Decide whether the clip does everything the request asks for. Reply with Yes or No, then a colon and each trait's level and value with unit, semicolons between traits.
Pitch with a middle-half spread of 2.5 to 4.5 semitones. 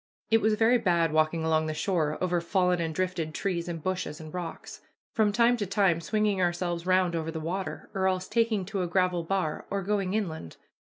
Yes: average, 3.1 semitones